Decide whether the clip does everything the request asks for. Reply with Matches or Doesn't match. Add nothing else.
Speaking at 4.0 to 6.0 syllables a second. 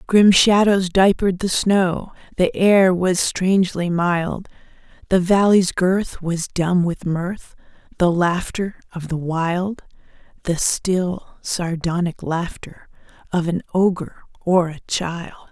Doesn't match